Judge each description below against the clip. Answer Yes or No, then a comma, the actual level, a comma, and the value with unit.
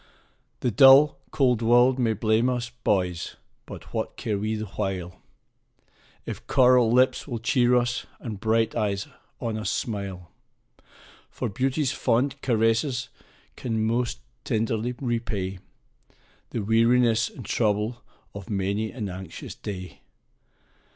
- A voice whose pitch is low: Yes, low, 115 Hz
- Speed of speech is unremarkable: No, slow, 125 wpm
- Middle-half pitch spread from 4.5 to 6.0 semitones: No, average, 3.1 semitones